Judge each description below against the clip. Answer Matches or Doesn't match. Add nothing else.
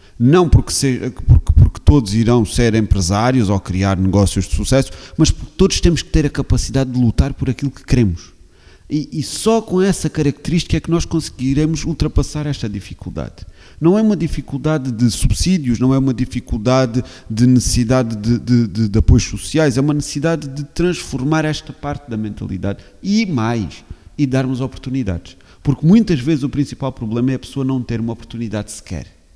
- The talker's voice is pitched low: Matches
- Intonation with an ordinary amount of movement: Doesn't match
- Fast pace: Doesn't match